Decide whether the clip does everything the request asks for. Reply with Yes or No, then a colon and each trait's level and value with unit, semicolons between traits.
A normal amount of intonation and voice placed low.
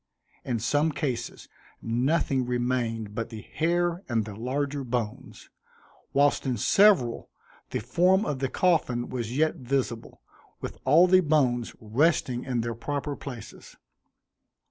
Yes: average, 4.1 semitones; low, 130 Hz